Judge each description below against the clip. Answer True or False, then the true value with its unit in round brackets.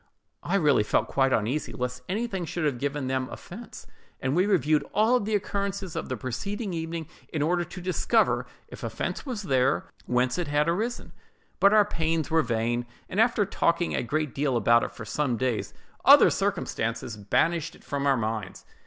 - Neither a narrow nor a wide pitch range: False (6.4 semitones)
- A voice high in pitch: False (150 Hz)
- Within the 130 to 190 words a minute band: True (180 wpm)